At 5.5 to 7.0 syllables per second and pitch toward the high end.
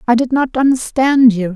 No: 5.0 syllables/s; high, 245 Hz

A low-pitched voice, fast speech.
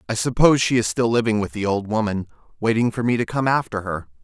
Yes: low, 110 Hz; fast, 240 wpm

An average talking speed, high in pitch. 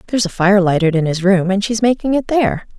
No: fast, 260 wpm; high, 200 Hz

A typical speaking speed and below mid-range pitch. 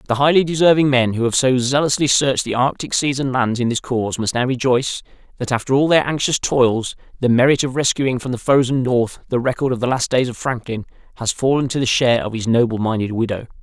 No: fast, 230 wpm; low, 125 Hz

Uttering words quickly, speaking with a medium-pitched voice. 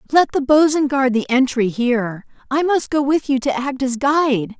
No: fast, 210 wpm; very high, 265 Hz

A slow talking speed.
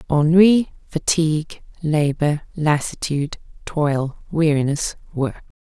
Yes: slow, 75 wpm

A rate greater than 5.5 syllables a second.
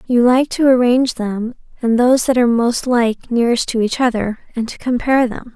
Yes: 5.7 syllables/s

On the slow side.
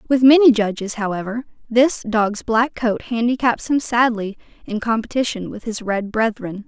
No: average, 155 wpm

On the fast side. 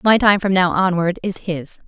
Yes: fast, 225 wpm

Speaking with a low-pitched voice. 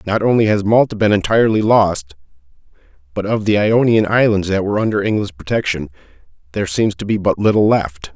Yes: low, 100 Hz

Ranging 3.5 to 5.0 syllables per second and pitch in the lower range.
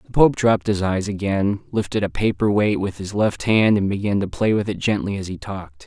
No: 5.5 syllables/s; low, 100 Hz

